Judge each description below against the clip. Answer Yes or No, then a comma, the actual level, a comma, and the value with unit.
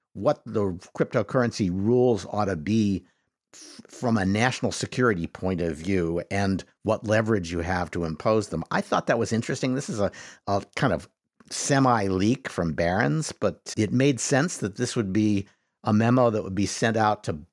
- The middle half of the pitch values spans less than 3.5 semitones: No, average, 4.2 semitones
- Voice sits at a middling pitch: No, low, 105 Hz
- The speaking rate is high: No, average, 185 wpm